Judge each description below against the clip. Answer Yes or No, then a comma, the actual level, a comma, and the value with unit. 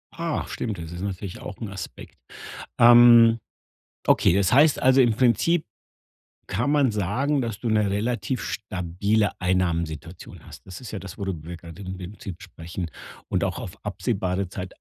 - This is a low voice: Yes, low, 100 Hz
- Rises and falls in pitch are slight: No, average, 4.6 semitones